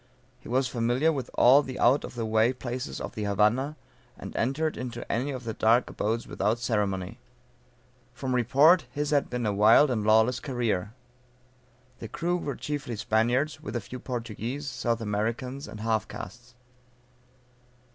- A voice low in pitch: Yes, low, 120 Hz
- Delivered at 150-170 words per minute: Yes, average, 160 wpm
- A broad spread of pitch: No, average, 3.1 semitones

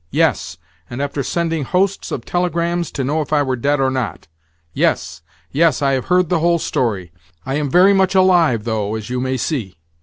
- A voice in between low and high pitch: Yes, medium, 145 Hz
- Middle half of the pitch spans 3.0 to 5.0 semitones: No, wide, 5.4 semitones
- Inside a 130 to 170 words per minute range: No, average, 200 wpm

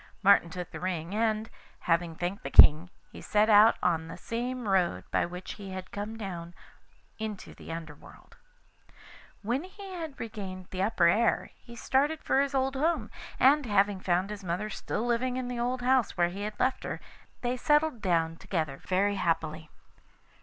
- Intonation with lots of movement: Yes, wide, 5.7 semitones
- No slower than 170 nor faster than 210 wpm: Yes, average, 180 wpm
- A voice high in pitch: Yes, high, 205 Hz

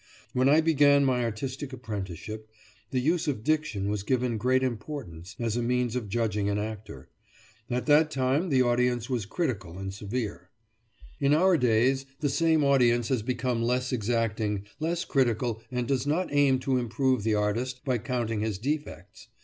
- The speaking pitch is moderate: No, low, 125 Hz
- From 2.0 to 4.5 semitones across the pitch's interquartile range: Yes, average, 3.8 semitones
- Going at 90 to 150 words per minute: No, average, 165 wpm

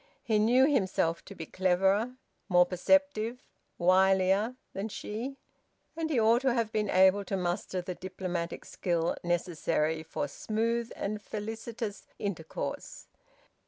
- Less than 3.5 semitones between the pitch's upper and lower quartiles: No, average, 4.2 semitones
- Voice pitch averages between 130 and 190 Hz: No, high, 200 Hz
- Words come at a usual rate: No, slow, 125 wpm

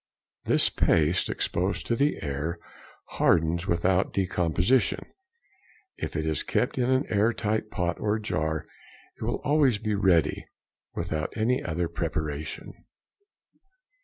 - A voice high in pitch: No, very low, 90 Hz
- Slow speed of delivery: Yes, slow, 125 wpm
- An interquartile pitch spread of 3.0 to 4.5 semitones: No, average, 5.2 semitones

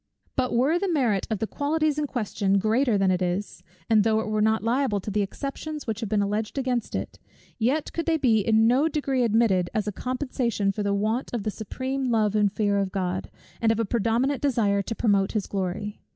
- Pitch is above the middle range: Yes, high, 220 Hz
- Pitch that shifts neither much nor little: Yes, average, 4.2 semitones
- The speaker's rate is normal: No, fast, 220 wpm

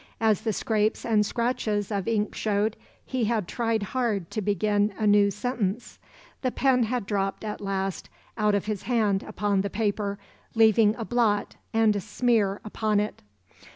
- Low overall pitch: No, high, 210 Hz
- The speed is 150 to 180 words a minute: Yes, average, 165 wpm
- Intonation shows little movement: Yes, narrow, 1.8 semitones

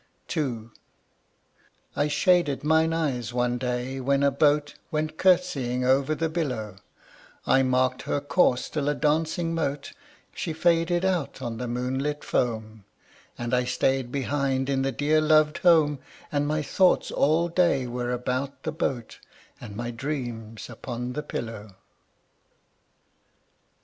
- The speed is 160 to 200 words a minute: No, slow, 135 wpm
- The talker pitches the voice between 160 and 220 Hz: No, medium, 140 Hz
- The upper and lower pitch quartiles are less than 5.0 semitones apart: Yes, average, 3.9 semitones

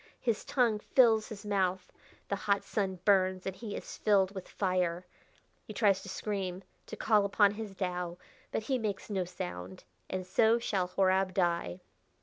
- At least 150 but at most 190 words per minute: Yes, average, 165 wpm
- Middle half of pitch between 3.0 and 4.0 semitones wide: No, narrow, 2.4 semitones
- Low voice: No, high, 195 Hz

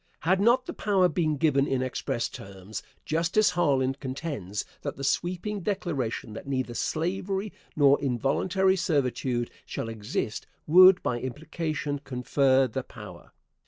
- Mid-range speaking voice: Yes, medium, 145 Hz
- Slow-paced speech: Yes, slow, 130 wpm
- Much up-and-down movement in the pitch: Yes, wide, 5.8 semitones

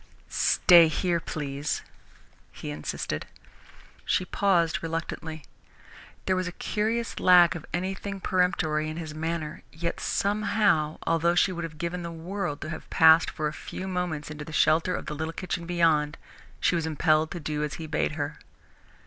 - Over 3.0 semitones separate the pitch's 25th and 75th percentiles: No, average, 2.7 semitones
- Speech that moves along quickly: No, average, 165 wpm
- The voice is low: No, medium, 165 Hz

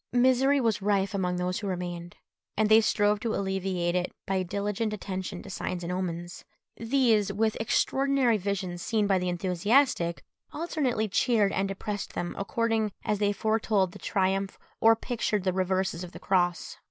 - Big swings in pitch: No, average, 3.3 semitones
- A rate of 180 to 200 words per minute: No, average, 165 wpm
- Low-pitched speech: No, high, 200 Hz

